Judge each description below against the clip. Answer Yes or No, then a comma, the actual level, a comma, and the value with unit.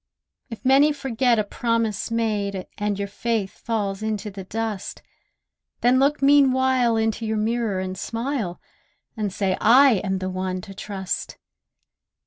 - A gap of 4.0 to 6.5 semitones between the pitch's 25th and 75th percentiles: No, average, 3.5 semitones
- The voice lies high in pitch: Yes, high, 220 Hz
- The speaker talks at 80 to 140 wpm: Yes, slow, 135 wpm